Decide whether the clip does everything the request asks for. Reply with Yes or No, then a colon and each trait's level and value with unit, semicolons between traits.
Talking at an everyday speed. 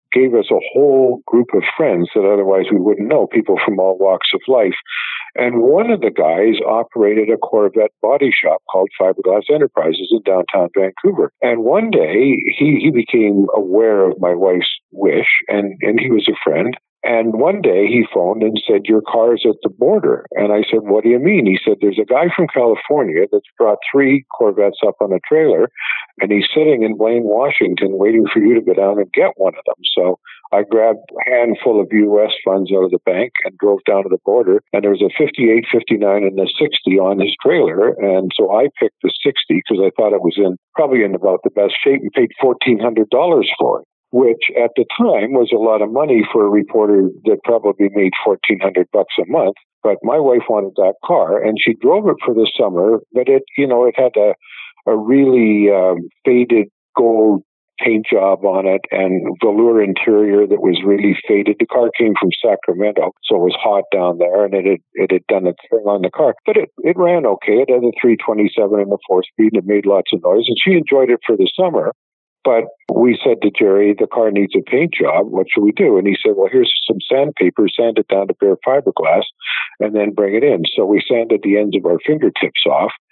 No: fast, 220 wpm